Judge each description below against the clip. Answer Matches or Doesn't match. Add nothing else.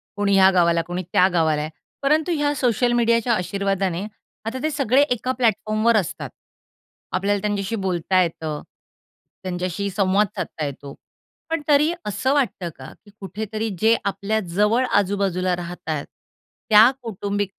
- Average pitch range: Matches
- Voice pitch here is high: Matches